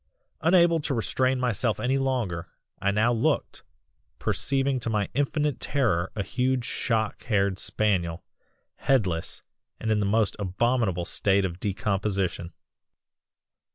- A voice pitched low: Yes, low, 110 Hz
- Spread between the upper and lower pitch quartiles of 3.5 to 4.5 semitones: No, average, 4.9 semitones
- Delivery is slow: Yes, slow, 120 wpm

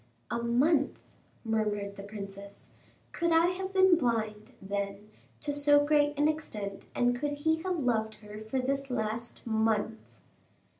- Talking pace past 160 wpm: No, average, 145 wpm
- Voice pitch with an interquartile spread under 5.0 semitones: No, wide, 5.5 semitones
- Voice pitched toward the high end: Yes, high, 235 Hz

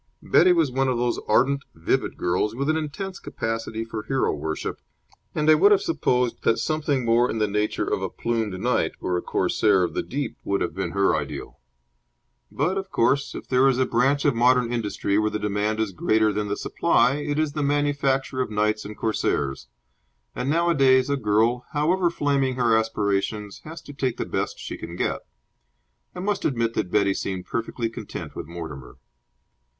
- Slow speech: No, average, 190 wpm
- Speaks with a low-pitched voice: Yes, low, 120 Hz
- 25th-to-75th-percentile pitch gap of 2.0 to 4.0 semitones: No, average, 5.2 semitones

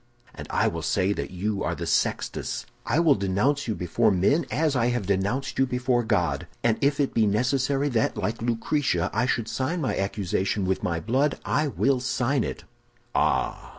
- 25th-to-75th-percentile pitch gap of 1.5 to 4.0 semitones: No, wide, 5.4 semitones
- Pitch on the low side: Yes, low, 120 Hz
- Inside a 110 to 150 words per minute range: No, average, 185 wpm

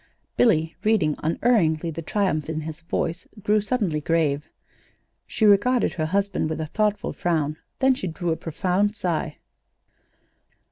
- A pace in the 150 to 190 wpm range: No, average, 140 wpm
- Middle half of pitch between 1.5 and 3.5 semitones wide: No, average, 4.7 semitones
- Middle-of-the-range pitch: Yes, medium, 170 Hz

